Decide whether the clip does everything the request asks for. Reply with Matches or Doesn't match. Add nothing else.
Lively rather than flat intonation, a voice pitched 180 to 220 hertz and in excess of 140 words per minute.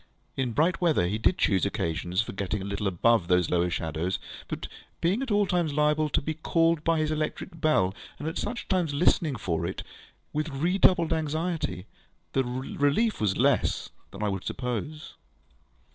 Doesn't match